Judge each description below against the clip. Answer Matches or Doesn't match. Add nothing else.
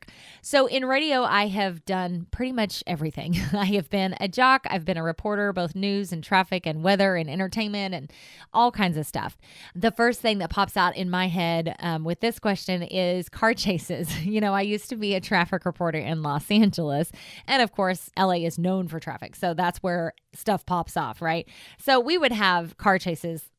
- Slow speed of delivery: Doesn't match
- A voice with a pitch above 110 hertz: Matches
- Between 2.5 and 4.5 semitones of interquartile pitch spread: Matches